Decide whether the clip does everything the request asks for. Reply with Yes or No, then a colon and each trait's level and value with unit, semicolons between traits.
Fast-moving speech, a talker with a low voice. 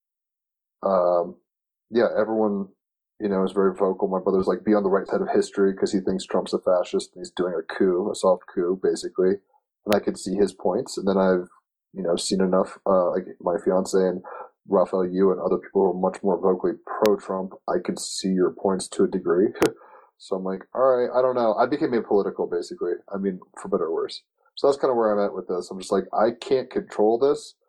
Yes: fast, 225 wpm; low, 120 Hz